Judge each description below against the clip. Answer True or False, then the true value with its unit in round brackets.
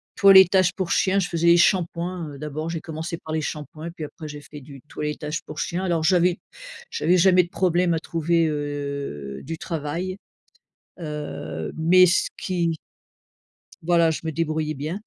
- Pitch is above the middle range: False (165 Hz)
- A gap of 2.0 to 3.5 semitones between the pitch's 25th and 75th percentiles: True (2.8 semitones)